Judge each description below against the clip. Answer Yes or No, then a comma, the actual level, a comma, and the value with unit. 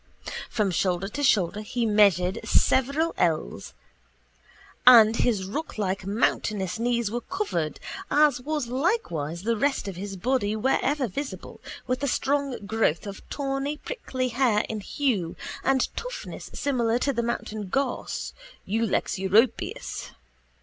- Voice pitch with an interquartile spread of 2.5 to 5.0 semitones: No, wide, 5.4 semitones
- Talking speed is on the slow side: Yes, slow, 130 wpm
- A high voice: Yes, high, 230 Hz